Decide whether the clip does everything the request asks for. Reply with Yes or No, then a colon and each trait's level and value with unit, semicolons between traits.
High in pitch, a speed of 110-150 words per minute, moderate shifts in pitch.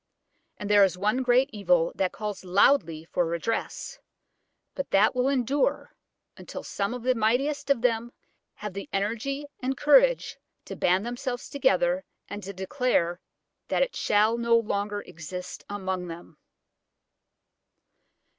Yes: high, 210 Hz; slow, 135 wpm; average, 5.0 semitones